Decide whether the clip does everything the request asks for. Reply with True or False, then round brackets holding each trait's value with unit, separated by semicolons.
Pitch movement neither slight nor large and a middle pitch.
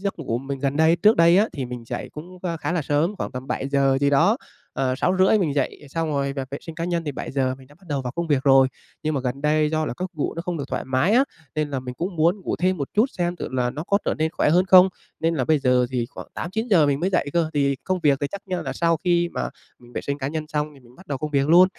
True (4.2 semitones; 150 Hz)